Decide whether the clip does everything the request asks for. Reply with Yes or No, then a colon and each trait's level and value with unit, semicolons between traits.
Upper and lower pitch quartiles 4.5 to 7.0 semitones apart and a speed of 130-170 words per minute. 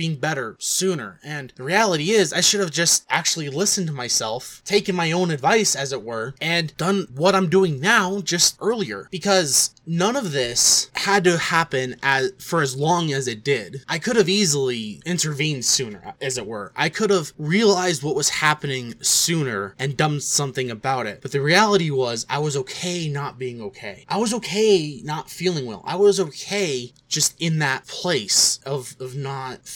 No: wide, 5.6 semitones; average, 185 wpm